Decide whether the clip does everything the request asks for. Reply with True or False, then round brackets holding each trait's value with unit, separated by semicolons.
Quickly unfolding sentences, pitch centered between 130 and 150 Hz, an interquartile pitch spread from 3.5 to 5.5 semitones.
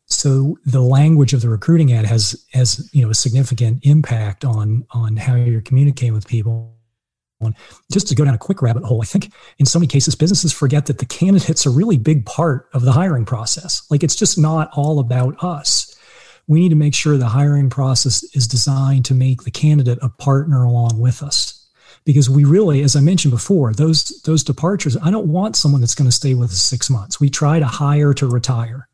True (215 wpm; 140 Hz; 3.9 semitones)